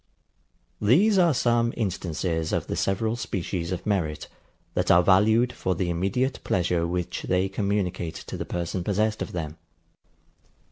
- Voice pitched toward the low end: Yes, very low, 95 Hz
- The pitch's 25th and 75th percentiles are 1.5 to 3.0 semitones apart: No, average, 4.1 semitones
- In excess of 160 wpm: No, average, 145 wpm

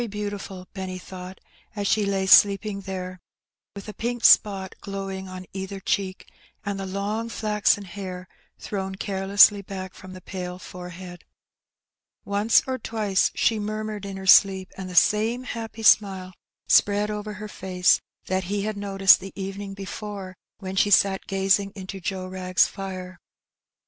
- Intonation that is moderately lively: No, narrow, 1.6 semitones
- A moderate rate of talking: Yes, average, 155 wpm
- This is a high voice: Yes, high, 195 Hz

